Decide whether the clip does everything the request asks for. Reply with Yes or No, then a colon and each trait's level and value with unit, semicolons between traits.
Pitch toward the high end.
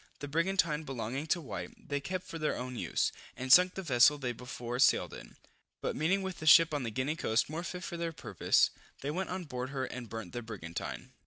No: medium, 140 Hz